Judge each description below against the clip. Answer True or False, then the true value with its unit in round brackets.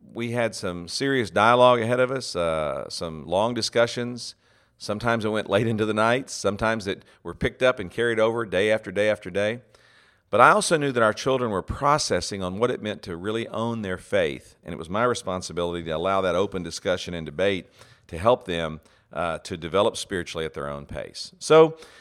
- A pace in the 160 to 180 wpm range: False (200 wpm)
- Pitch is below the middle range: True (110 Hz)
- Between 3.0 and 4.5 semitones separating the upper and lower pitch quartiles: True (4.1 semitones)